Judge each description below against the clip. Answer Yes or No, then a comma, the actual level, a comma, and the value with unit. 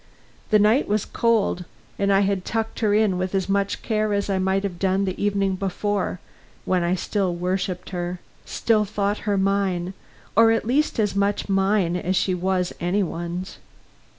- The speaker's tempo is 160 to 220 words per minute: Yes, average, 180 wpm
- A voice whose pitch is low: No, high, 195 Hz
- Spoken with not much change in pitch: Yes, narrow, 2.0 semitones